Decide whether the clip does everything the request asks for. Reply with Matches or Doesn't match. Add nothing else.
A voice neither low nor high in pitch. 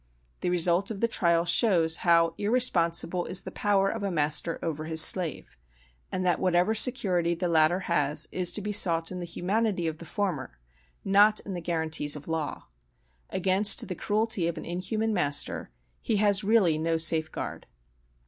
Matches